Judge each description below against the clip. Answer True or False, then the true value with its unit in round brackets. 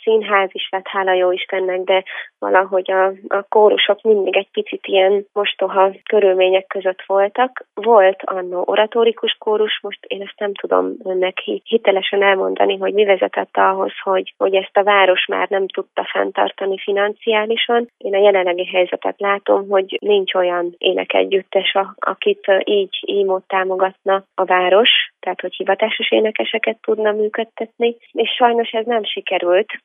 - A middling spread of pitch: False (2.2 semitones)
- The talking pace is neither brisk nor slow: True (145 wpm)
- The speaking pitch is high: True (195 Hz)